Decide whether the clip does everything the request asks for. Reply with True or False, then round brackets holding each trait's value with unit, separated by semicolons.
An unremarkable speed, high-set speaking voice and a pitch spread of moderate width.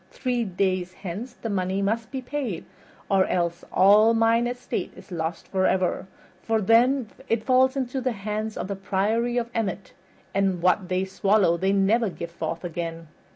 True (165 wpm; 200 Hz; 3.8 semitones)